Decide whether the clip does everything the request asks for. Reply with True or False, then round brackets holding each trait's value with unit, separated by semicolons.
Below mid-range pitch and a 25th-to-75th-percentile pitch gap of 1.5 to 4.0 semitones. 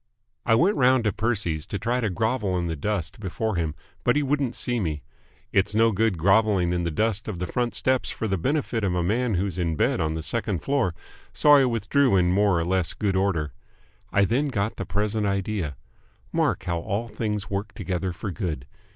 False (100 Hz; 4.4 semitones)